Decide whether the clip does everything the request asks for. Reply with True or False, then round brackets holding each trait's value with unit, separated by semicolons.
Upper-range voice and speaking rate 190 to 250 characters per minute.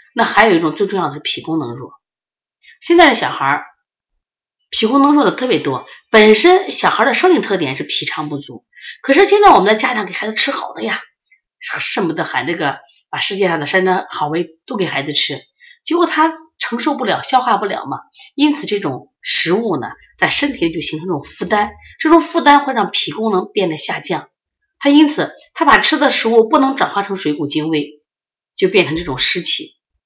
False (225 Hz; 290 characters per minute)